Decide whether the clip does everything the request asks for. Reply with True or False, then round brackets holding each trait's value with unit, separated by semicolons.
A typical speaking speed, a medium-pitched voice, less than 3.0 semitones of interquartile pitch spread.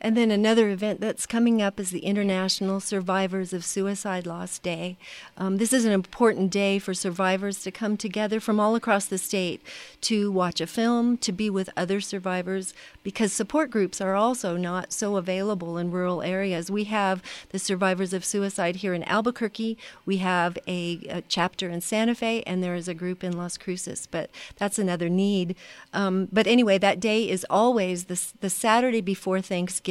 False (185 wpm; 195 Hz; 2.6 semitones)